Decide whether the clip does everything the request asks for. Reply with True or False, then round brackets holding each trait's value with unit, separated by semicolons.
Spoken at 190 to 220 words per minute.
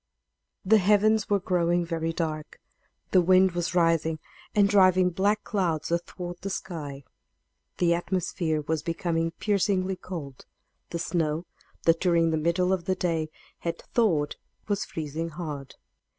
False (135 wpm)